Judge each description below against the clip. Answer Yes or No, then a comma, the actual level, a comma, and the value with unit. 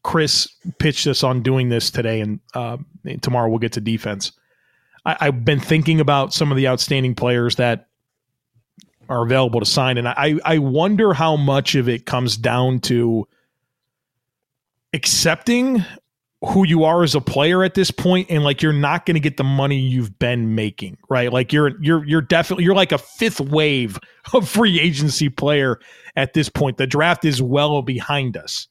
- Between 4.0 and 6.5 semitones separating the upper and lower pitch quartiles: Yes, average, 4.4 semitones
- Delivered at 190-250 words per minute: No, average, 180 wpm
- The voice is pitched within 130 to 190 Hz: Yes, medium, 140 Hz